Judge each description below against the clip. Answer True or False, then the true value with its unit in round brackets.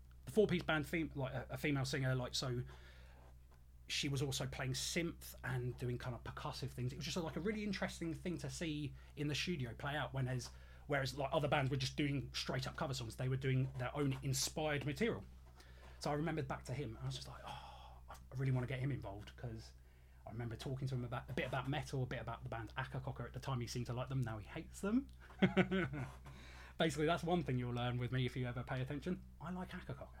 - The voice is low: True (130 Hz)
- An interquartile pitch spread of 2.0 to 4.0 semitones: True (3.7 semitones)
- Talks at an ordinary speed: False (235 wpm)